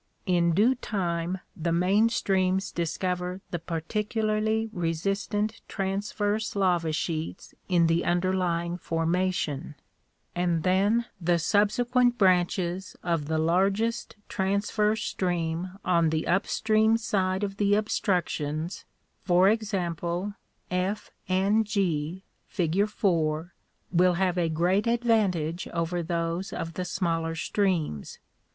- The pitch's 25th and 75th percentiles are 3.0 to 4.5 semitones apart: Yes, average, 3.3 semitones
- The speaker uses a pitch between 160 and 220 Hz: Yes, medium, 185 Hz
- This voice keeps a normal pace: No, slow, 115 wpm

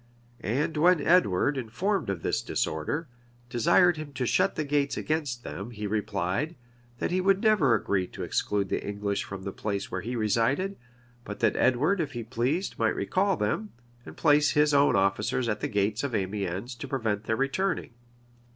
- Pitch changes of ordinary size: No, wide, 6.9 semitones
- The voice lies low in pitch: Yes, low, 125 Hz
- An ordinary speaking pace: Yes, average, 180 wpm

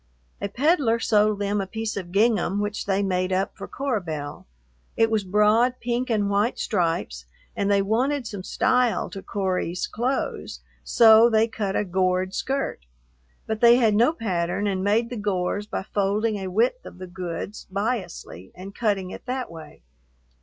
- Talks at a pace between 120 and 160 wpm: No, average, 170 wpm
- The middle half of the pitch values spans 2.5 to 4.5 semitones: Yes, average, 3.5 semitones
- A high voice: Yes, high, 205 Hz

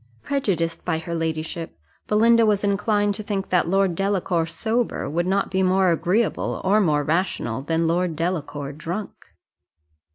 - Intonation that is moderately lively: Yes, average, 3.8 semitones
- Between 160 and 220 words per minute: No, average, 150 wpm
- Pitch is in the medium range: Yes, medium, 180 Hz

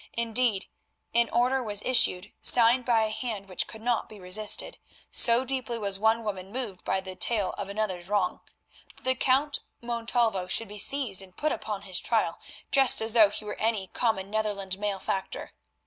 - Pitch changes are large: No, average, 3.3 semitones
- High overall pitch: Yes, high, 215 Hz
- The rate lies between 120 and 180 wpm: Yes, average, 170 wpm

